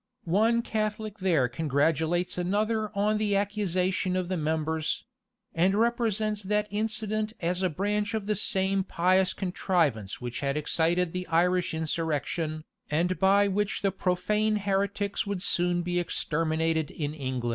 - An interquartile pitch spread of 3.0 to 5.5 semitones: Yes, average, 4.1 semitones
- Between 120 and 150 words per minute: Yes, average, 140 wpm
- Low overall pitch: No, medium, 185 Hz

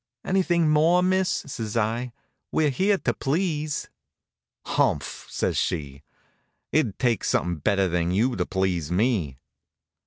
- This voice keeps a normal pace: No, slow, 125 wpm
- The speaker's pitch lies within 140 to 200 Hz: No, low, 120 Hz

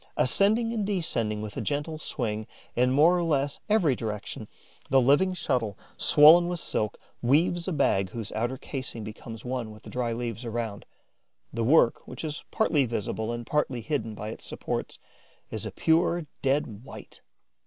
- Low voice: Yes, low, 130 Hz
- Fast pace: No, average, 165 wpm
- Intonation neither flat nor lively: No, wide, 5.9 semitones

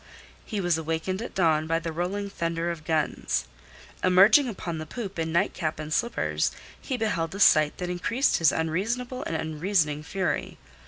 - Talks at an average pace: Yes, average, 165 wpm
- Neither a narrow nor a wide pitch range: Yes, average, 3.8 semitones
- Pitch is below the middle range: No, medium, 170 Hz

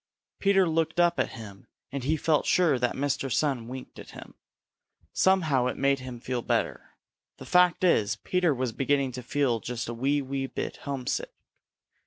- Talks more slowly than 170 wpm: No, average, 175 wpm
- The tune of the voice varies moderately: Yes, average, 4.3 semitones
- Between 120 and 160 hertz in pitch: Yes, low, 135 Hz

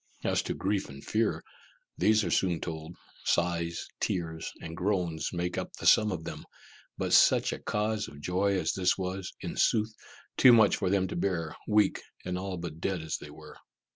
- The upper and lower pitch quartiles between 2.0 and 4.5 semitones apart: Yes, average, 3.1 semitones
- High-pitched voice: No, very low, 90 Hz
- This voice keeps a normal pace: Yes, average, 190 wpm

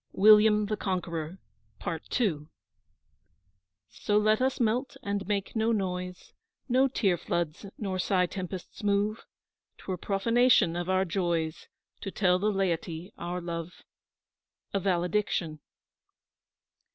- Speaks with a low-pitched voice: No, high, 190 Hz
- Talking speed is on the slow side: Yes, slow, 115 wpm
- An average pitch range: Yes, average, 3.3 semitones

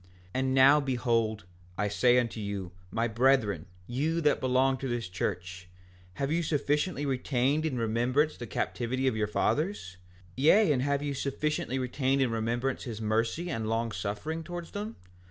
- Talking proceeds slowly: No, average, 165 wpm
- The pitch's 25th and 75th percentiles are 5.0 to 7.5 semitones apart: No, average, 4.2 semitones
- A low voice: Yes, low, 130 Hz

